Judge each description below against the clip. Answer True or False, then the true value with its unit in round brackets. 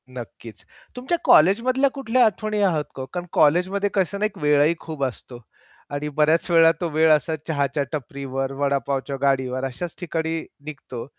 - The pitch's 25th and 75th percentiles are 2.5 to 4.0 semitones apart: False (5.1 semitones)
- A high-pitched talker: False (155 Hz)